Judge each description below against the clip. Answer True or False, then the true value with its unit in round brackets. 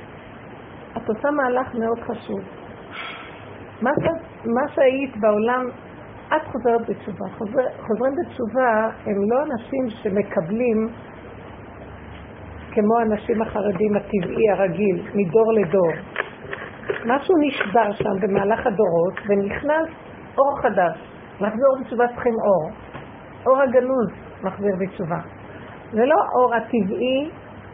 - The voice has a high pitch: True (225 Hz)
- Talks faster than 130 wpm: False (105 wpm)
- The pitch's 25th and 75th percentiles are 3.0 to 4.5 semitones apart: True (4.1 semitones)